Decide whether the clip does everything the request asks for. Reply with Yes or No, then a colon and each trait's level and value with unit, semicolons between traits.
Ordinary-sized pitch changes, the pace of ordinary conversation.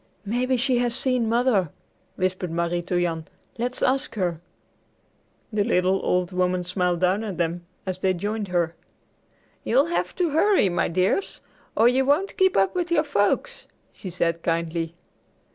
No: wide, 6.2 semitones; average, 160 wpm